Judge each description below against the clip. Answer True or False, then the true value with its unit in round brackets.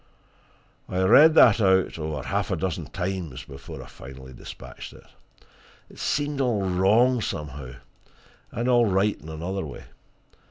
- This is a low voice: True (95 Hz)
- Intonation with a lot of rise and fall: True (7.0 semitones)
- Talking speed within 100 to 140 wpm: True (135 wpm)